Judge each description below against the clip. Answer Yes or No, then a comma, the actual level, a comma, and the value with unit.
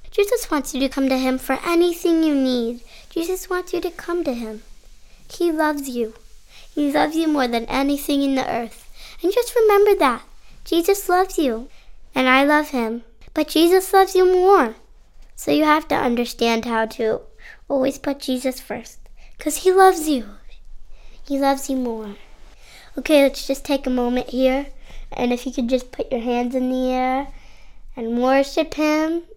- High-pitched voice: Yes, very high, 275 Hz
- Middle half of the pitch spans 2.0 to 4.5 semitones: No, average, 5.1 semitones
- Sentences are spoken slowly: No, average, 175 wpm